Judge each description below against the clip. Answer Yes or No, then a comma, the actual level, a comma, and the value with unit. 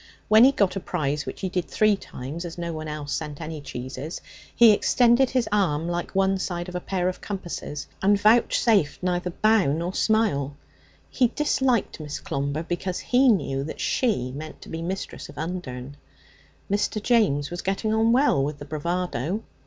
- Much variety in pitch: Yes, wide, 6.1 semitones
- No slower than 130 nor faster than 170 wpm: No, average, 180 wpm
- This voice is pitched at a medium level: Yes, medium, 180 Hz